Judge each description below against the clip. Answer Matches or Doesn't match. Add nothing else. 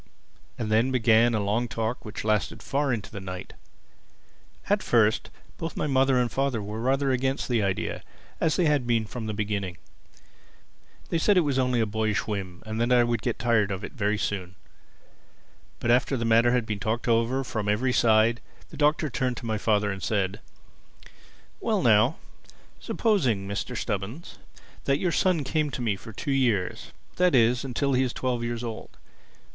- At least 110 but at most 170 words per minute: Doesn't match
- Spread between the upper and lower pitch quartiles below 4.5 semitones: Matches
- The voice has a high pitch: Doesn't match